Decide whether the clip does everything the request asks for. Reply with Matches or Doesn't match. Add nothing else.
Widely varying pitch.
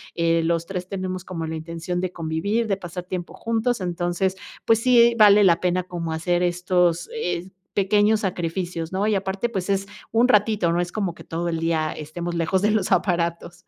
Doesn't match